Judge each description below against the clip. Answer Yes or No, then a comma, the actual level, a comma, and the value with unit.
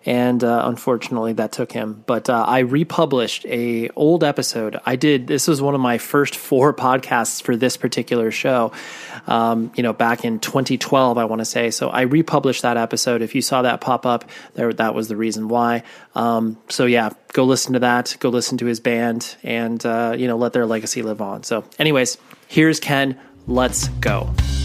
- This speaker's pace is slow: No, average, 195 wpm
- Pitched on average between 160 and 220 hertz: No, low, 120 Hz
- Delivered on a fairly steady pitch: Yes, narrow, 2.3 semitones